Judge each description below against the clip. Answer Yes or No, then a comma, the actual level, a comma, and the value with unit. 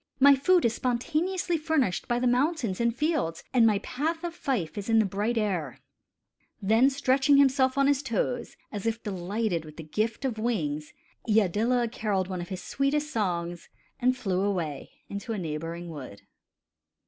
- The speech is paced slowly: No, average, 170 wpm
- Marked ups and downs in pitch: Yes, wide, 6.3 semitones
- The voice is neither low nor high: No, high, 225 Hz